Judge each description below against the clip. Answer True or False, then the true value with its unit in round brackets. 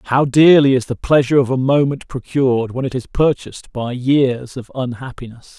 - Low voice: True (130 Hz)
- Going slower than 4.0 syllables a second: False (5.1 syllables/s)